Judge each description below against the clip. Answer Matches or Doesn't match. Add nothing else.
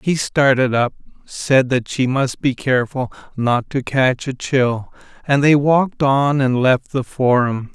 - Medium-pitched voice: Doesn't match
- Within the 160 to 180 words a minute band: Matches